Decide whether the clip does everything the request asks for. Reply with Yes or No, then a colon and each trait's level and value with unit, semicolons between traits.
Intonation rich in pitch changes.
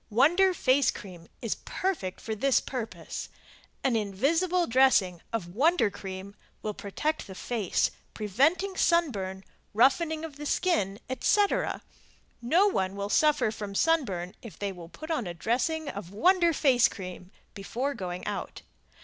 Yes: wide, 8.2 semitones